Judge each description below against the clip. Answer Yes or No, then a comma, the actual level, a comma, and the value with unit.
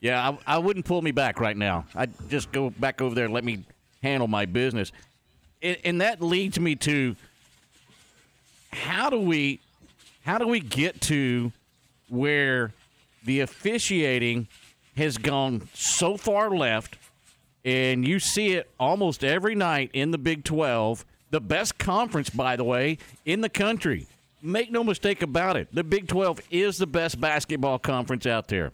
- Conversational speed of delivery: Yes, average, 165 wpm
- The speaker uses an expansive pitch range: Yes, wide, 5.8 semitones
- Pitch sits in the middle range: Yes, medium, 145 Hz